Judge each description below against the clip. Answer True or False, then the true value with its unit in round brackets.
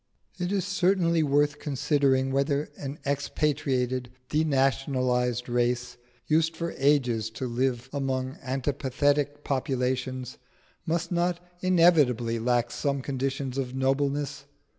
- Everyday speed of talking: False (105 wpm)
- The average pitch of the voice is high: False (135 Hz)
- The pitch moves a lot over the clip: False (2.6 semitones)